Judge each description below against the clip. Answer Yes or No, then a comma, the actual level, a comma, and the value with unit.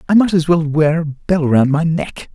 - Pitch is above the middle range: No, medium, 160 Hz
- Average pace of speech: No, fast, 255 wpm